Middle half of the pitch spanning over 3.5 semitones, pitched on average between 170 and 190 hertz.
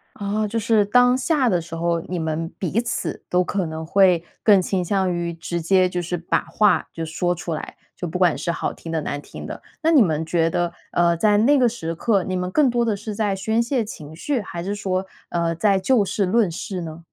Yes: average, 4.1 semitones; medium, 185 Hz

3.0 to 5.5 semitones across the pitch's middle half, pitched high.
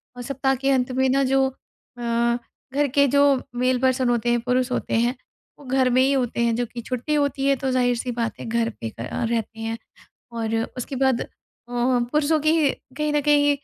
No: narrow, 2.4 semitones; very high, 255 Hz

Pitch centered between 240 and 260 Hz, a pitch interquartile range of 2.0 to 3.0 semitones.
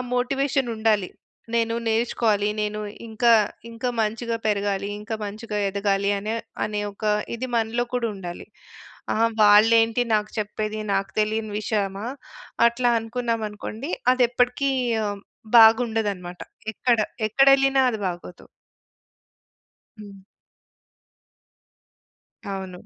No: high, 220 Hz; narrow, 2.4 semitones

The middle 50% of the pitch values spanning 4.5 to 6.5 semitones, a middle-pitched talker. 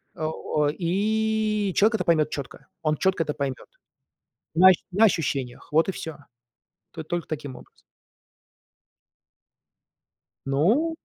Yes: average, 5.3 semitones; medium, 165 Hz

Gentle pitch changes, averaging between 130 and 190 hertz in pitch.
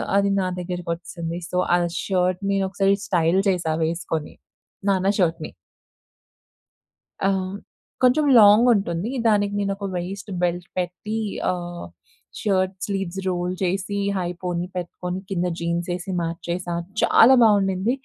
Yes: narrow, 2.2 semitones; medium, 185 Hz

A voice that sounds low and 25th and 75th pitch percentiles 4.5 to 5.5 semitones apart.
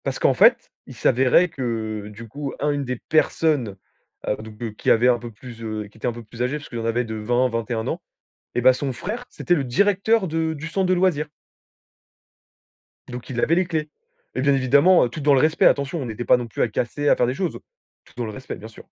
Yes: low, 125 Hz; average, 4.9 semitones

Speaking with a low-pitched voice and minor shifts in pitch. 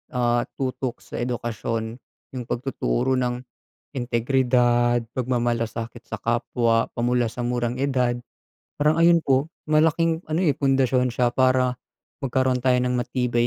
Yes: low, 125 Hz; narrow, 1.7 semitones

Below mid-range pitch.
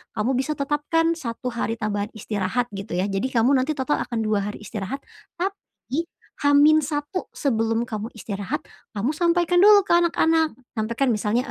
No: very high, 255 Hz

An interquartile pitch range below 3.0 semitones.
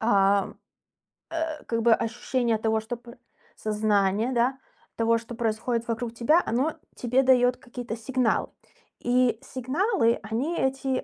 Yes: narrow, 2.5 semitones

